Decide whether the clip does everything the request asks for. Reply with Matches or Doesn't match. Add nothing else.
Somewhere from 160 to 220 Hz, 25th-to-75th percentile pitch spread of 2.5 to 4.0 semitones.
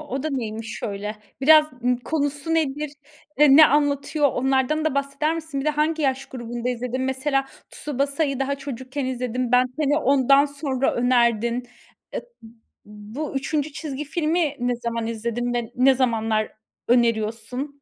Doesn't match